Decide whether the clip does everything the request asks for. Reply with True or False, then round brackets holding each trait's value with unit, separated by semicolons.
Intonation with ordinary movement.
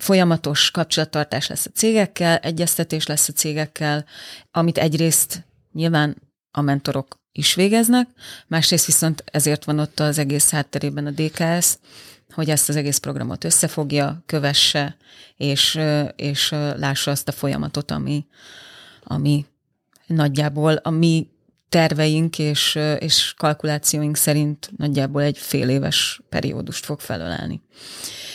False (2.1 semitones)